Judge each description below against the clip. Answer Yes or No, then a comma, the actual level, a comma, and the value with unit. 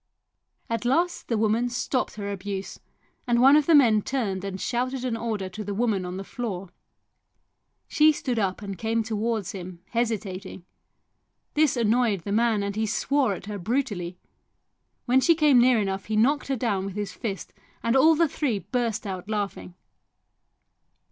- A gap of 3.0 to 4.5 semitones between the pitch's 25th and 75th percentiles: Yes, average, 4.1 semitones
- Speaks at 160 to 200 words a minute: Yes, average, 170 wpm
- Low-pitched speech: No, high, 220 Hz